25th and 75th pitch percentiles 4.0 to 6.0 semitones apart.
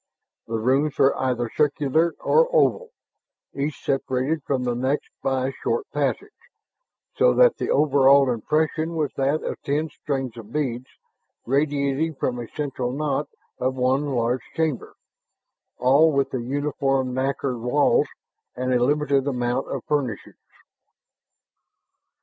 No: average, 2.7 semitones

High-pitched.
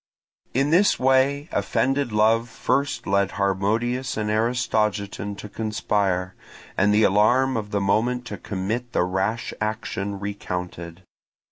No: low, 105 Hz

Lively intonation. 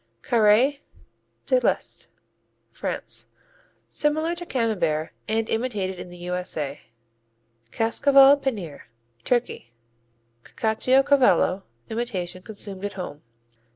Yes: wide, 6.4 semitones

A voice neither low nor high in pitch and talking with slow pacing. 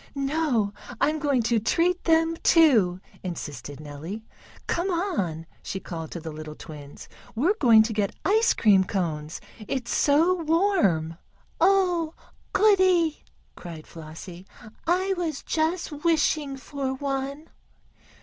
No: very high, 275 Hz; slow, 120 wpm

